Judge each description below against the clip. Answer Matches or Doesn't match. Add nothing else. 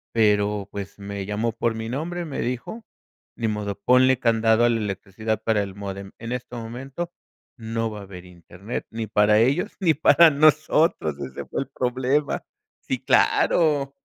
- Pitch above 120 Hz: Doesn't match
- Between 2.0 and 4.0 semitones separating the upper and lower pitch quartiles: Doesn't match